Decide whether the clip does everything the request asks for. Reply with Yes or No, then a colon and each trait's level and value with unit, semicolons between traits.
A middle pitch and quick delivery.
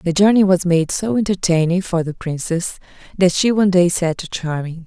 No: medium, 175 Hz; average, 195 wpm